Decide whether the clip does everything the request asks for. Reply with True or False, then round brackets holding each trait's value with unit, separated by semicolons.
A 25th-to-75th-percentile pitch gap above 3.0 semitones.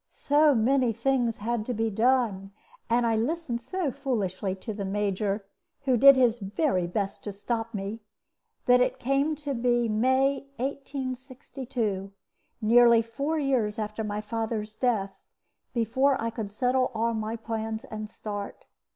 True (3.5 semitones)